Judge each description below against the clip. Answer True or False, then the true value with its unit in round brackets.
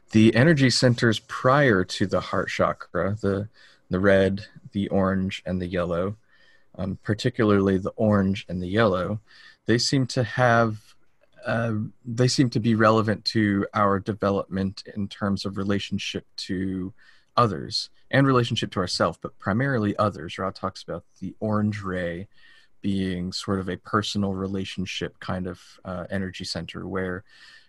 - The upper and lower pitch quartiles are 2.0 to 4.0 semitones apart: True (2.9 semitones)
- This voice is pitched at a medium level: False (100 Hz)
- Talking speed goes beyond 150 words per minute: False (145 wpm)